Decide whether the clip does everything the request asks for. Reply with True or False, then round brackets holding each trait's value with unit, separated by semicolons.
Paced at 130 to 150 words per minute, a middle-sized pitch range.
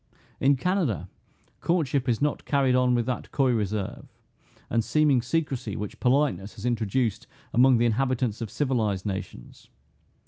True (140 wpm; 3.9 semitones)